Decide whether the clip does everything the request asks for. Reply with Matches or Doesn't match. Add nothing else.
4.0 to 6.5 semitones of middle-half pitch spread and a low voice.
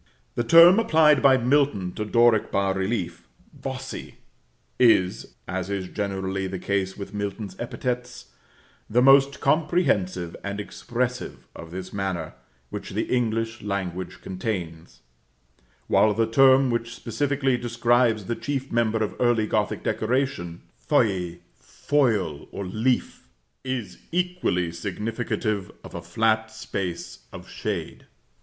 Matches